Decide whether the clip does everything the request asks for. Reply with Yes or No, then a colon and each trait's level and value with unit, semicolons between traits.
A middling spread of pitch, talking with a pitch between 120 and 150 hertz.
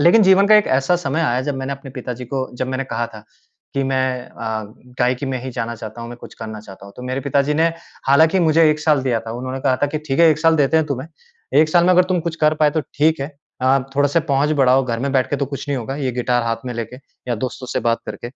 Yes: average, 3.5 semitones; low, 135 Hz